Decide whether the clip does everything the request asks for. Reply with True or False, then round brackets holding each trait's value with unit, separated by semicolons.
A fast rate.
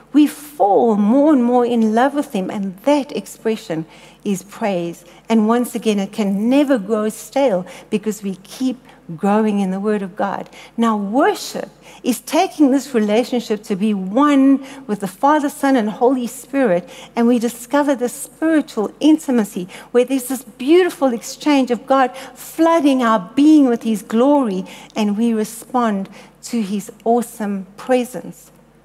False (150 wpm)